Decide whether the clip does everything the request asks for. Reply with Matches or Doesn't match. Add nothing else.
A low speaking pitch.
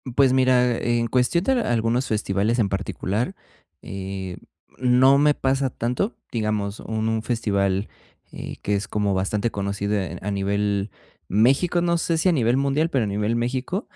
Matches